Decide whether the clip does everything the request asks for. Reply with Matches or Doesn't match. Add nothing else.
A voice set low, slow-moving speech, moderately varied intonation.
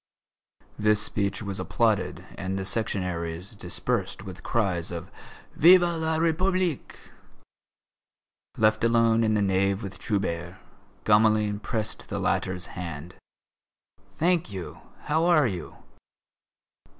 Matches